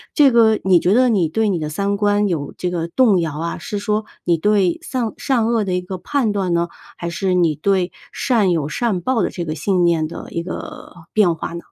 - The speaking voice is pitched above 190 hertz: No, medium, 185 Hz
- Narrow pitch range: No, average, 4.1 semitones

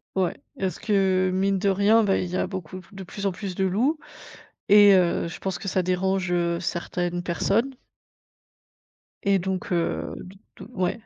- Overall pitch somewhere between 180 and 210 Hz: Yes, high, 190 Hz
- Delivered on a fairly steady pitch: Yes, narrow, 1.7 semitones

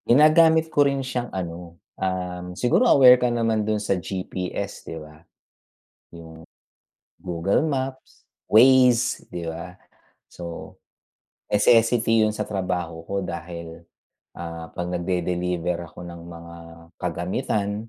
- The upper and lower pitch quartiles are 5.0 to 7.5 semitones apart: Yes, wide, 5.6 semitones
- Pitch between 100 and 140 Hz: No, very low, 90 Hz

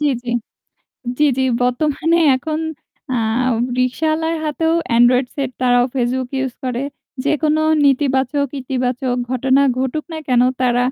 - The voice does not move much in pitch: No, average, 3.2 semitones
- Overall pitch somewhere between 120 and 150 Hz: No, very high, 260 Hz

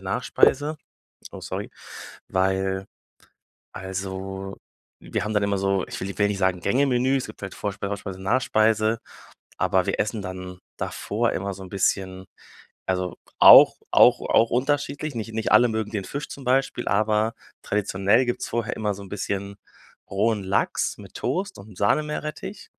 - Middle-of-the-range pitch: No, low, 100 Hz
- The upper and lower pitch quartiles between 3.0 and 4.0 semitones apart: Yes, average, 3.4 semitones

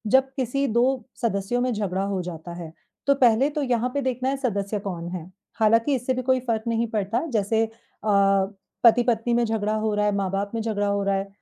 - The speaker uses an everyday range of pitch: Yes, average, 3.7 semitones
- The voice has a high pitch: Yes, high, 225 Hz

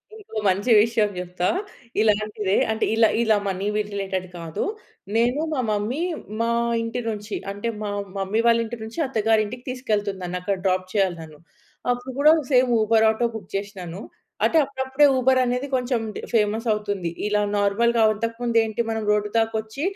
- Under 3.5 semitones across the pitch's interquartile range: Yes, average, 2.8 semitones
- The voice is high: Yes, high, 220 Hz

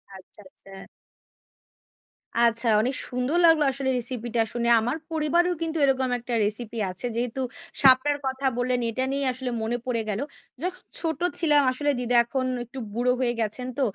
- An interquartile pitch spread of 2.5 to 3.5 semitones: Yes, average, 2.9 semitones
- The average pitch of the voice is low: No, very high, 255 Hz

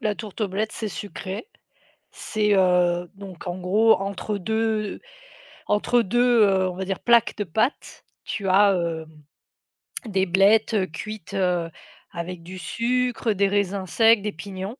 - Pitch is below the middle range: No, high, 200 Hz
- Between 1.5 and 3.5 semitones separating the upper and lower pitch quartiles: Yes, average, 2.9 semitones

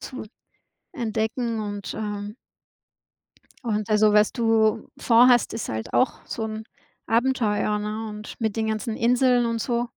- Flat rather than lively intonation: Yes, narrow, 1.9 semitones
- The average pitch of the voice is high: Yes, high, 220 Hz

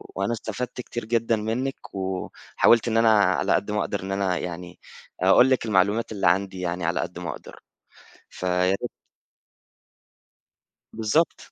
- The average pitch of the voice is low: Yes, low, 100 Hz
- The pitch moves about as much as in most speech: Yes, average, 3.8 semitones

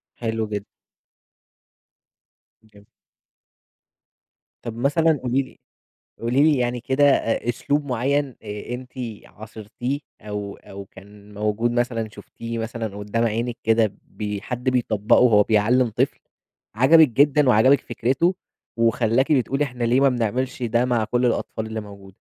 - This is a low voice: Yes, low, 115 Hz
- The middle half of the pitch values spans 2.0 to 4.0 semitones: Yes, average, 3.2 semitones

